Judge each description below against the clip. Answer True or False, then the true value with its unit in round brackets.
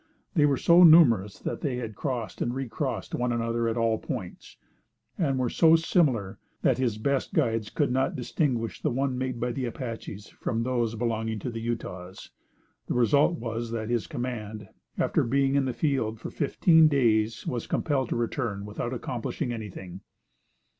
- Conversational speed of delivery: True (165 wpm)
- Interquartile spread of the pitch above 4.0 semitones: False (3.2 semitones)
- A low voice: True (120 Hz)